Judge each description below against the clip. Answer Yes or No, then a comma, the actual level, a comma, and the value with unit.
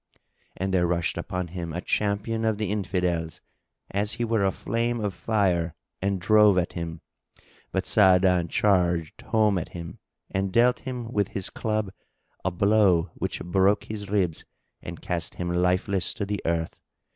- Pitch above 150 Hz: No, very low, 95 Hz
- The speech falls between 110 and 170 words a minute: Yes, average, 160 wpm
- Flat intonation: No, average, 3.1 semitones